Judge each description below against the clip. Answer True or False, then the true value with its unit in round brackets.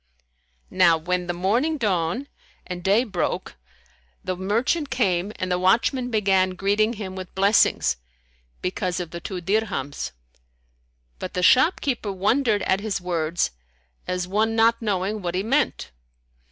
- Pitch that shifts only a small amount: False (3.7 semitones)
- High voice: True (195 Hz)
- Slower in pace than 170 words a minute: True (140 wpm)